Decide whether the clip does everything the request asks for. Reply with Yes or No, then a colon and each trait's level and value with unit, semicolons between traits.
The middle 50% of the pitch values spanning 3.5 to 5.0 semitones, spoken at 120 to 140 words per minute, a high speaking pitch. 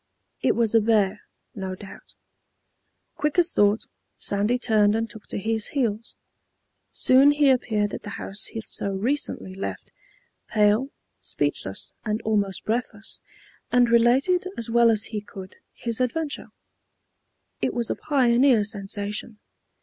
No: average, 3.1 semitones; slow, 135 wpm; high, 225 Hz